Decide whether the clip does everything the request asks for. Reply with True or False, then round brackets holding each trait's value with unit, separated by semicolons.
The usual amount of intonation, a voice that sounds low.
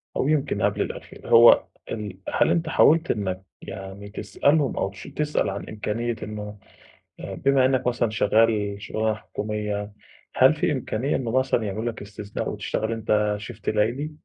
True (4.0 semitones; 110 Hz)